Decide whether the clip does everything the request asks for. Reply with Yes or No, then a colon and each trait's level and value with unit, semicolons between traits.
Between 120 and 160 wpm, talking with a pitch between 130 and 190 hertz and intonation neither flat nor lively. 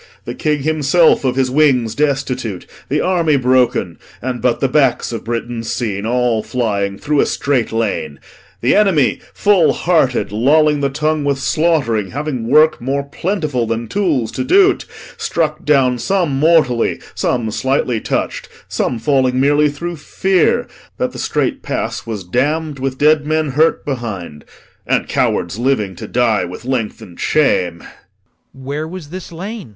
Yes: average, 155 wpm; low, 135 Hz; average, 4.7 semitones